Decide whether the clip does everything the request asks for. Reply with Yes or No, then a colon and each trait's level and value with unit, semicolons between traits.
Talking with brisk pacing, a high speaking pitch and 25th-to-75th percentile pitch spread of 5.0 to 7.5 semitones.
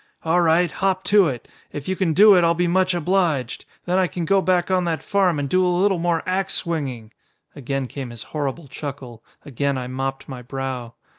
No: fast, 210 wpm; medium, 165 Hz; average, 5.3 semitones